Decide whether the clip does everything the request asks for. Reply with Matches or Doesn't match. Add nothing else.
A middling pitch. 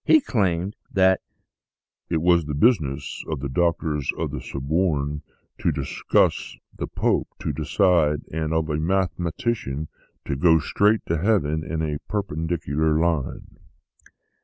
Doesn't match